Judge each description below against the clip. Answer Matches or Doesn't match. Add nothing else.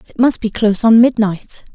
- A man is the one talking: Doesn't match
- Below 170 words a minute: Doesn't match